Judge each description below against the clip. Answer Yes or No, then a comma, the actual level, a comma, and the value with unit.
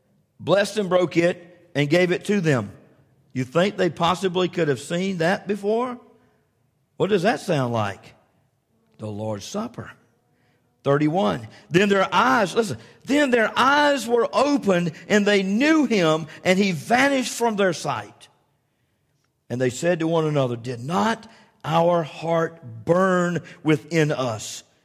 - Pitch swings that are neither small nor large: No, wide, 6.4 semitones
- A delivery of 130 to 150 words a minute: Yes, average, 140 wpm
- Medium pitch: Yes, medium, 170 Hz